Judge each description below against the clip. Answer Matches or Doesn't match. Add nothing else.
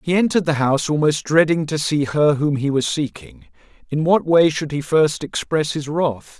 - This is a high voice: Doesn't match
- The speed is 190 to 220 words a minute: Matches